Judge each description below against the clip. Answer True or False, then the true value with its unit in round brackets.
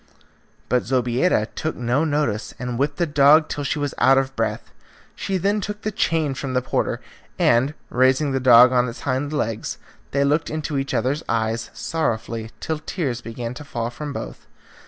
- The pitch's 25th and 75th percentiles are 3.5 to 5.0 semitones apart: True (3.9 semitones)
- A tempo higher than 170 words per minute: True (180 wpm)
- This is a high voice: False (135 Hz)